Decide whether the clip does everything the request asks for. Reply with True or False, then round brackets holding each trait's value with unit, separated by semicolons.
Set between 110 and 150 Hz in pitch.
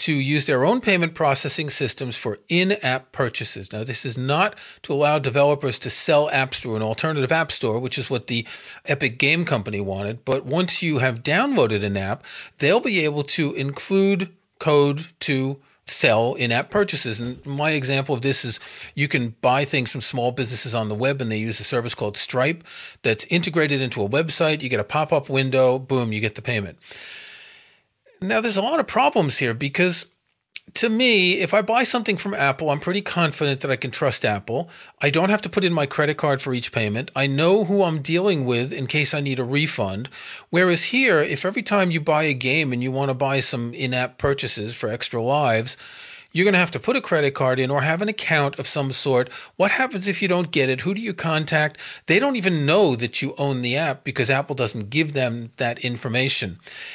True (140 Hz)